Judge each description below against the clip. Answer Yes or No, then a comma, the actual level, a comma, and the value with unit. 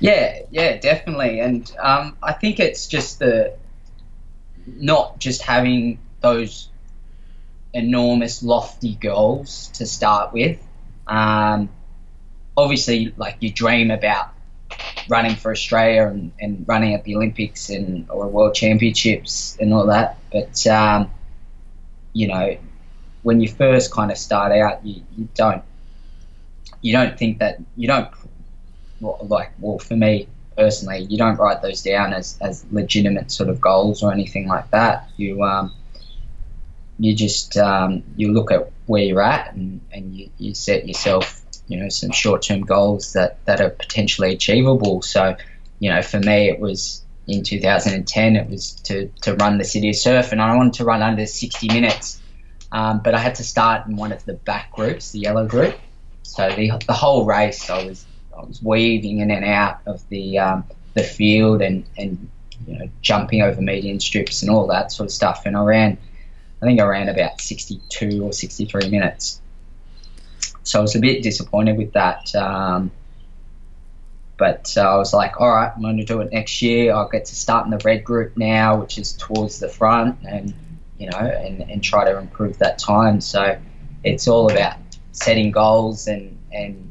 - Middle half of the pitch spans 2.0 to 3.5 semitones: Yes, narrow, 2.4 semitones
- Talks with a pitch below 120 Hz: Yes, low, 105 Hz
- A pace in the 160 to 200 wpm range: Yes, average, 175 wpm